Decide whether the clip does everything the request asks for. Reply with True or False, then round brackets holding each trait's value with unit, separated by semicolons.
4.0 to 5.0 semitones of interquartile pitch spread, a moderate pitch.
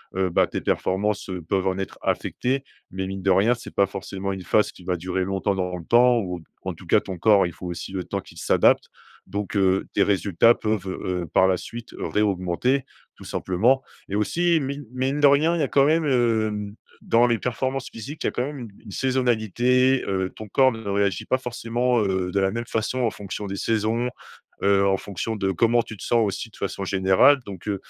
False (4.4 semitones; 105 Hz)